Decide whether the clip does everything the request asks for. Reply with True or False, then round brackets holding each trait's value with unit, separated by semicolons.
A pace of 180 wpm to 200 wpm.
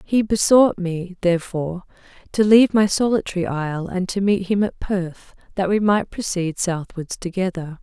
False (160 wpm)